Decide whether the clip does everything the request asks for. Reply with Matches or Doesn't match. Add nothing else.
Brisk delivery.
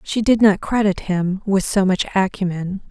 Doesn't match